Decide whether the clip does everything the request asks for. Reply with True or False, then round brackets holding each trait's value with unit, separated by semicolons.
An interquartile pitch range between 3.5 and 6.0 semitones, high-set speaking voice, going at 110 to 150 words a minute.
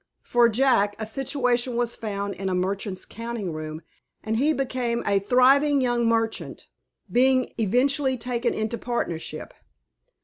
True (3.8 semitones; 235 Hz; 135 wpm)